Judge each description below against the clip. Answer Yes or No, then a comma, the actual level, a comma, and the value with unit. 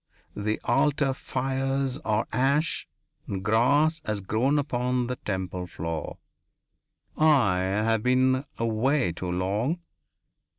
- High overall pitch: No, low, 125 Hz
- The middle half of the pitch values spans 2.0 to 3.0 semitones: No, average, 4.9 semitones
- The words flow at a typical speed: No, slow, 110 wpm